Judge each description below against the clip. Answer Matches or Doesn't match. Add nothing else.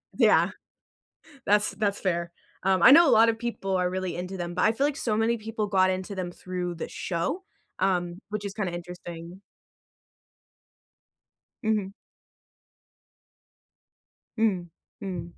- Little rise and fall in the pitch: Doesn't match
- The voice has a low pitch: Doesn't match